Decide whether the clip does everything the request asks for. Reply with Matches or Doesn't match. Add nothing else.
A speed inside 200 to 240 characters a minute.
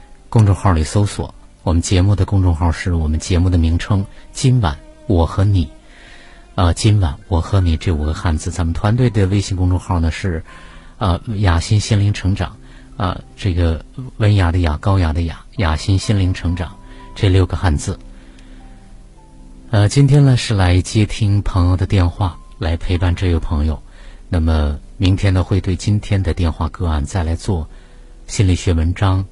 Doesn't match